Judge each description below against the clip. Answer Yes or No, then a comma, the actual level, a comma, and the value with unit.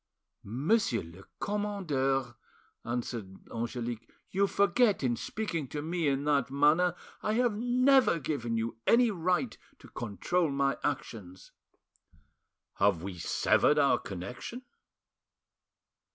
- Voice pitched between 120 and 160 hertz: Yes, medium, 140 Hz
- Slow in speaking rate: Yes, slow, 110 wpm